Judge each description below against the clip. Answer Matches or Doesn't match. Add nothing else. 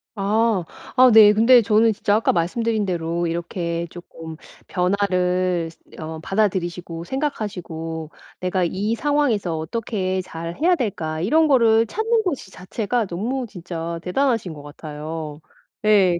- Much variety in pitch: Doesn't match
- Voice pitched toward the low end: Doesn't match